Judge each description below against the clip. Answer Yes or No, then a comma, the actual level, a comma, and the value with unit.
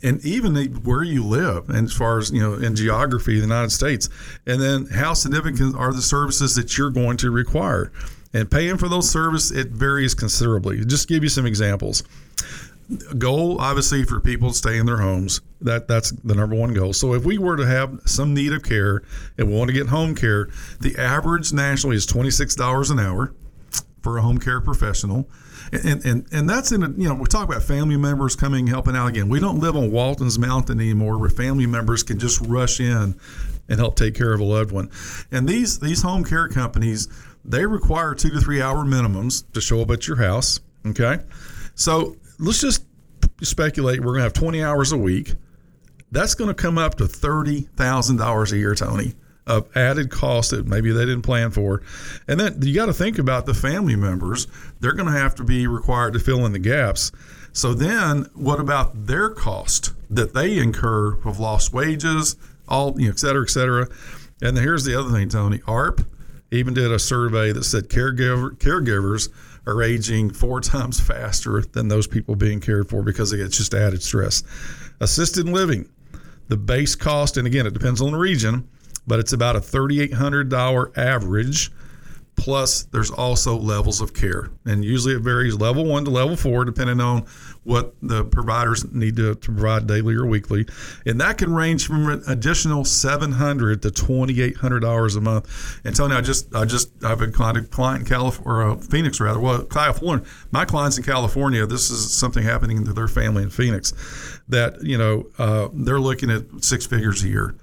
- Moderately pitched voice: No, low, 125 Hz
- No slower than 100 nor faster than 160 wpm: No, average, 195 wpm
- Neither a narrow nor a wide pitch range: Yes, average, 3.9 semitones